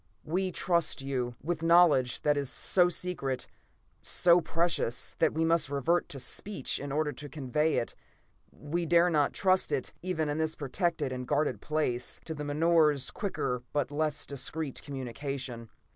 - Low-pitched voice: No, medium, 150 Hz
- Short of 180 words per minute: Yes, average, 160 wpm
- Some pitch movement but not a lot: Yes, average, 3.7 semitones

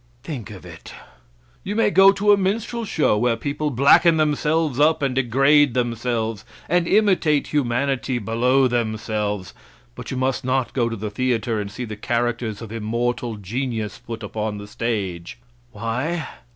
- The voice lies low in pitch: Yes, low, 120 Hz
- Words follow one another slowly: No, average, 160 wpm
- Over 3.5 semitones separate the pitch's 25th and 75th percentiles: Yes, average, 4.7 semitones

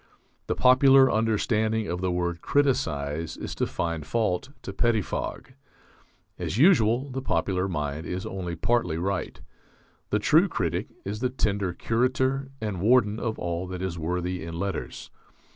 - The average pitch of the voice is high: No, low, 100 Hz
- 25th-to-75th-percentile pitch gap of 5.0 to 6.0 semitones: Yes, wide, 5.6 semitones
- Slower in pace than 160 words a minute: Yes, average, 145 wpm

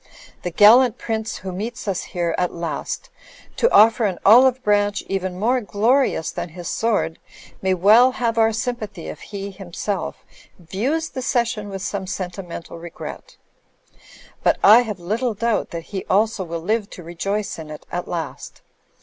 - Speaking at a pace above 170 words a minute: No, average, 160 wpm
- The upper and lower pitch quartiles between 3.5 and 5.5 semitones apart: Yes, average, 4.3 semitones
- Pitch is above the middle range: Yes, high, 205 Hz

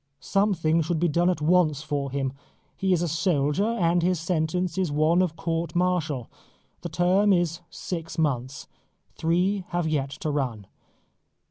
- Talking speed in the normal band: Yes, average, 155 wpm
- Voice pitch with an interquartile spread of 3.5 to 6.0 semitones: No, average, 3.1 semitones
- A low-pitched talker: No, medium, 165 Hz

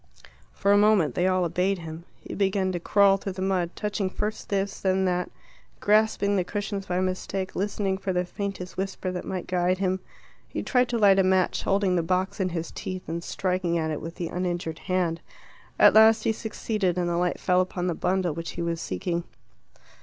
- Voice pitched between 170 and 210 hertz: Yes, medium, 185 Hz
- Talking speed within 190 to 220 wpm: Yes, fast, 205 wpm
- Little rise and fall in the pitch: Yes, narrow, 1.9 semitones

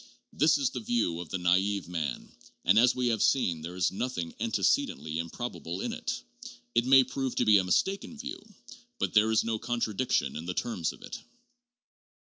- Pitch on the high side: No, low, 105 Hz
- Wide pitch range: Yes, wide, 6.0 semitones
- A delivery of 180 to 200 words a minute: Yes, average, 185 wpm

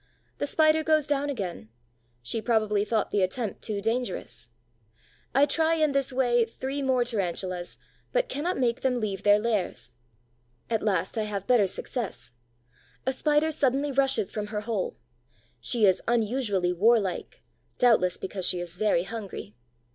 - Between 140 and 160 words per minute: Yes, average, 150 wpm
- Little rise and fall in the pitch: No, average, 5.3 semitones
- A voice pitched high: Yes, high, 225 Hz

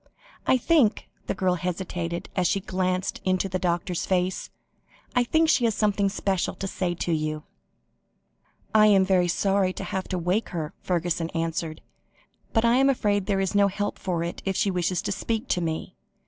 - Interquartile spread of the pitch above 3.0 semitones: No, narrow, 2.6 semitones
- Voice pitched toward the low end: No, medium, 185 Hz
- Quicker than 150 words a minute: Yes, average, 180 wpm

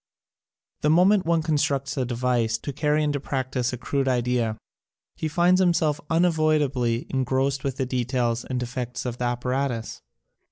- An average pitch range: Yes, average, 3.6 semitones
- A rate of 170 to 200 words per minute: No, average, 155 wpm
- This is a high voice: No, low, 135 Hz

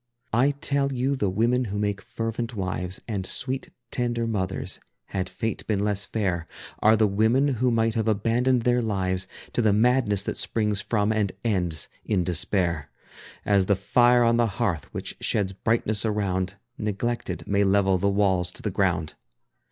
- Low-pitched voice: Yes, low, 105 Hz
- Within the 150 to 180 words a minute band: Yes, average, 165 wpm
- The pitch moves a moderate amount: Yes, average, 3.4 semitones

